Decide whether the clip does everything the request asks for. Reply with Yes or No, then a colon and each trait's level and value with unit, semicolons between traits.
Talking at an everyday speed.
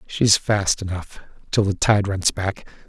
Yes: average, 165 wpm